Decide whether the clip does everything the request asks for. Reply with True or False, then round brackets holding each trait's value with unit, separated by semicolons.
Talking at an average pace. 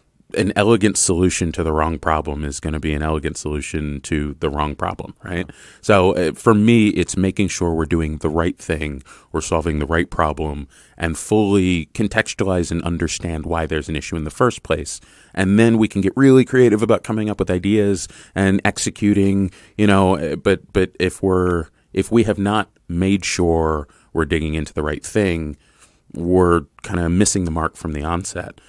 True (185 wpm)